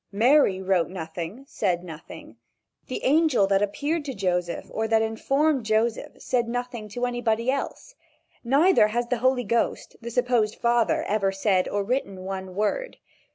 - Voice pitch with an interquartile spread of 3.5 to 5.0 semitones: Yes, average, 4.4 semitones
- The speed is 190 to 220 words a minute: No, average, 155 wpm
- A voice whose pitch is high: Yes, high, 225 Hz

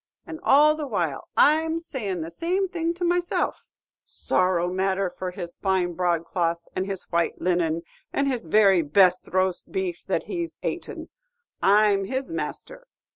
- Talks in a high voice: Yes, high, 195 Hz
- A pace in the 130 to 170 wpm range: Yes, average, 155 wpm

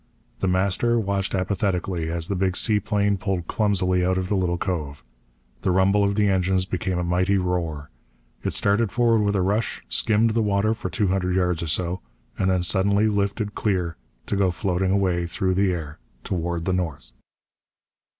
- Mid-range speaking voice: No, very low, 95 Hz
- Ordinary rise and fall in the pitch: No, narrow, 2.1 semitones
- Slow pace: No, average, 175 wpm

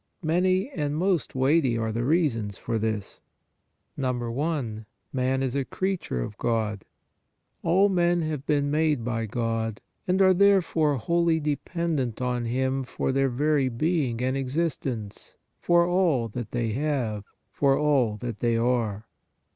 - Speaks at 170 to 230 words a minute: No, average, 145 wpm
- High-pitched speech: No, low, 135 Hz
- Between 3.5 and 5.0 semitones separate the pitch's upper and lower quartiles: No, wide, 5.6 semitones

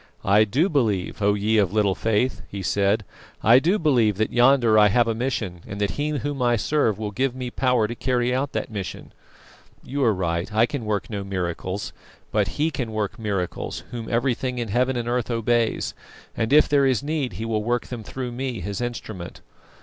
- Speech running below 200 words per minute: No, fast, 205 wpm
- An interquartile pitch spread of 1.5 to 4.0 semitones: Yes, average, 3.7 semitones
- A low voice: Yes, low, 115 Hz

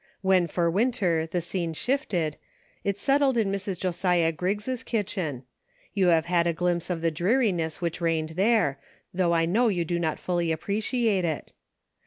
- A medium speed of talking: Yes, average, 165 wpm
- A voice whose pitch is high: No, medium, 180 Hz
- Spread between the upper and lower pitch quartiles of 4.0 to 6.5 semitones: No, average, 3.5 semitones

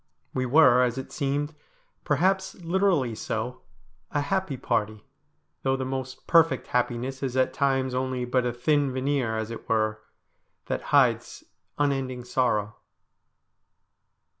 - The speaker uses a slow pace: Yes, slow, 130 wpm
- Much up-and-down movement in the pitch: No, average, 2.7 semitones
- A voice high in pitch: No, low, 130 Hz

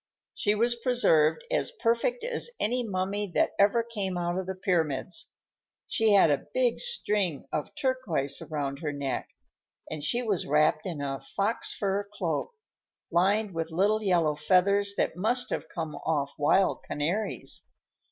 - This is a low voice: No, high, 190 Hz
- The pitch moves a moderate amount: No, wide, 5.8 semitones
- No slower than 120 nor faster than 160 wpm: Yes, average, 150 wpm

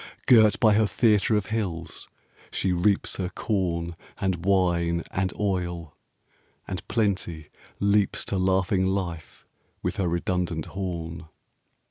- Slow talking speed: Yes, slow, 125 wpm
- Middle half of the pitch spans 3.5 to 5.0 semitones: No, average, 2.8 semitones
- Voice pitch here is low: Yes, very low, 95 Hz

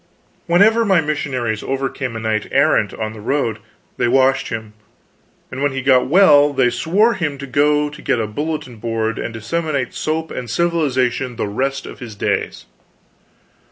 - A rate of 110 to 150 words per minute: No, average, 165 wpm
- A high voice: No, low, 135 Hz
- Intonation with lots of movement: No, average, 4.6 semitones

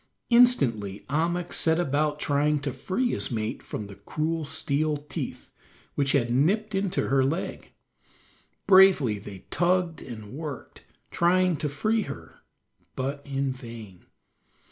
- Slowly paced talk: Yes, slow, 130 wpm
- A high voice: No, medium, 145 Hz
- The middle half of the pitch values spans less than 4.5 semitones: No, average, 5.3 semitones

